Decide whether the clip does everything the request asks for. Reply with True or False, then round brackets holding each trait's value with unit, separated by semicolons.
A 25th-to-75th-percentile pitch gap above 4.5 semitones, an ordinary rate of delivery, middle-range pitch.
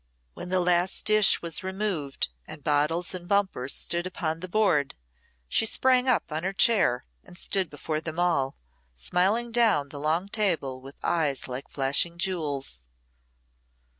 True (4.9 semitones; 150 wpm; 170 Hz)